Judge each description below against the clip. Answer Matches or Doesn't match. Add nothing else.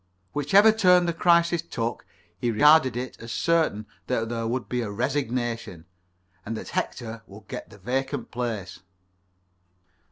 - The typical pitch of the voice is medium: Doesn't match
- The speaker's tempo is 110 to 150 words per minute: Matches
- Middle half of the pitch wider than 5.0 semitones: Matches